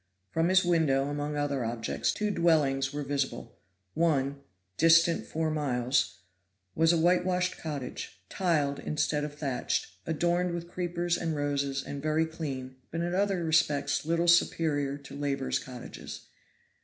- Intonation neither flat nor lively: Yes, average, 3.3 semitones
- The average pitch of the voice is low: No, medium, 150 Hz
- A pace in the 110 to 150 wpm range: Yes, average, 140 wpm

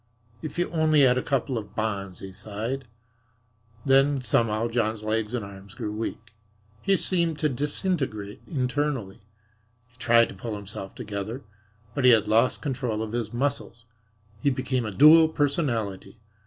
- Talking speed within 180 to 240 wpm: No, average, 155 wpm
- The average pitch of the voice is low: Yes, low, 120 Hz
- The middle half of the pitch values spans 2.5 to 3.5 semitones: No, average, 4.7 semitones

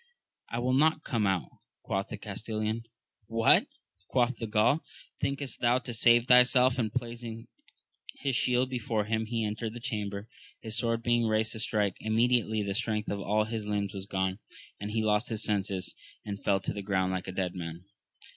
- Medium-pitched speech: No, low, 110 Hz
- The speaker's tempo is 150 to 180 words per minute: No, average, 190 wpm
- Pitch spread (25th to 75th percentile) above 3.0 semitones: No, average, 2.7 semitones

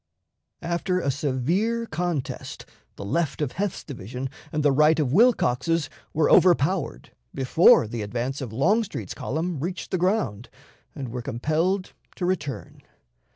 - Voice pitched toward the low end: No, medium, 155 Hz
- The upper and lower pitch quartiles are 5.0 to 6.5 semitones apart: Yes, wide, 5.6 semitones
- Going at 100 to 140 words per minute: Yes, slow, 135 wpm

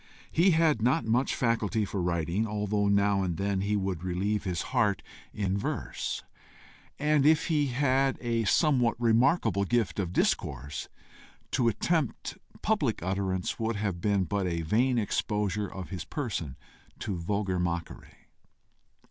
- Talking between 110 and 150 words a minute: Yes, average, 140 wpm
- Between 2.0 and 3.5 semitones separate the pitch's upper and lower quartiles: No, average, 4.4 semitones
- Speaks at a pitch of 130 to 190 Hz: No, low, 105 Hz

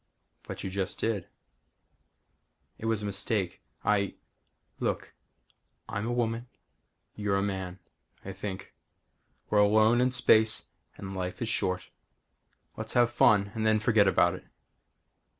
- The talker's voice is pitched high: No, low, 105 Hz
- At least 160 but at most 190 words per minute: No, slow, 135 wpm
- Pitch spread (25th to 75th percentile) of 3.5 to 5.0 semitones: No, narrow, 2.5 semitones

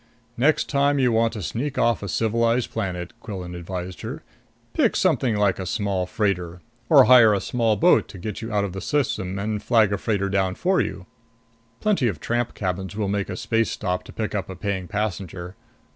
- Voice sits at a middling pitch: No, low, 105 Hz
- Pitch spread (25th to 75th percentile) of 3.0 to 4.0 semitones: Yes, average, 3.6 semitones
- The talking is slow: No, average, 200 wpm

